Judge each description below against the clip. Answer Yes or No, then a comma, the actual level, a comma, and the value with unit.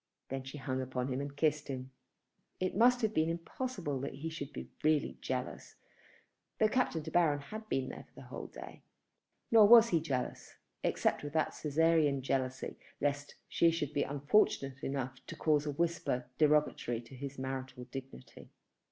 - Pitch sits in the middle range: Yes, medium, 145 Hz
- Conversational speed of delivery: Yes, average, 170 wpm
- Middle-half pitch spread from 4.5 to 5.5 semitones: No, average, 3.7 semitones